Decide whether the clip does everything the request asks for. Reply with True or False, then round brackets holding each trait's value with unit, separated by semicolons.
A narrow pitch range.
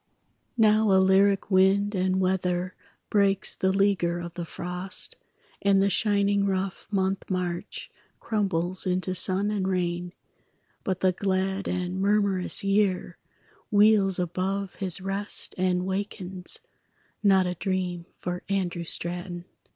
True (1.7 semitones)